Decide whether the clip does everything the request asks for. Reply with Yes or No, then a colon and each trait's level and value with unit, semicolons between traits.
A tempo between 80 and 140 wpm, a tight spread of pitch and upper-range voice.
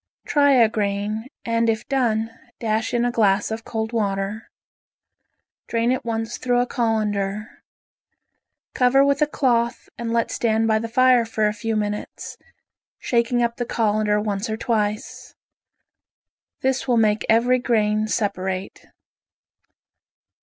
Yes: slow, 135 wpm; narrow, 2.1 semitones; high, 225 Hz